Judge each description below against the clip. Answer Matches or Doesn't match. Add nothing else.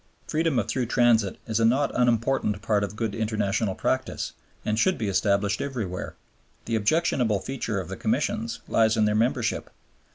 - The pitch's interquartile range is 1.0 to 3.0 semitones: Matches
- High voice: Doesn't match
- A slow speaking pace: Doesn't match